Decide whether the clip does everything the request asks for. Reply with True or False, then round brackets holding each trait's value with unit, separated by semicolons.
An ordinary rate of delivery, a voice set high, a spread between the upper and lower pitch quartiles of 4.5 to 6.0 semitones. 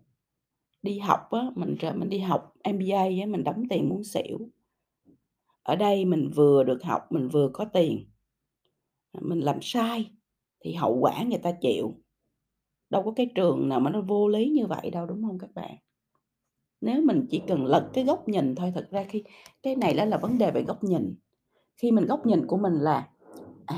True (200 wpm; 200 Hz; 5.0 semitones)